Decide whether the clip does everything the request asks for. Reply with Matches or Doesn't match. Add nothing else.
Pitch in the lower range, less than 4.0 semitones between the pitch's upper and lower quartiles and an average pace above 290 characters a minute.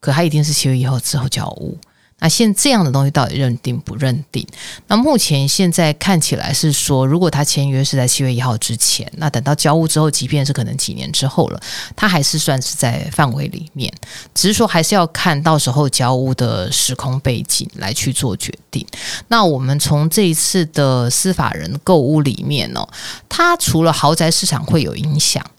Doesn't match